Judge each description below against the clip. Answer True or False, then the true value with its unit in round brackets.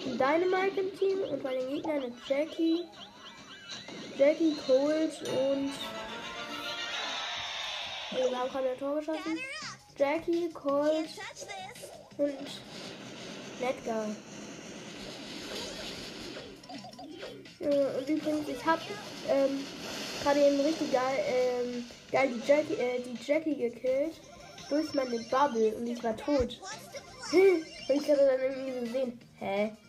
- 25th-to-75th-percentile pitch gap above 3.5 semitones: False (3.1 semitones)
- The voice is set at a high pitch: True (280 Hz)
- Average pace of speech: False (110 wpm)